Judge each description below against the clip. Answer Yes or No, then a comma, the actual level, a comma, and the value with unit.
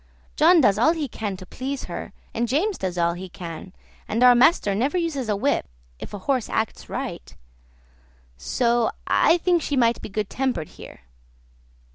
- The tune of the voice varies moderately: No, wide, 6.3 semitones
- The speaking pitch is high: Yes, high, 240 Hz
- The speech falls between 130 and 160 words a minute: No, average, 175 wpm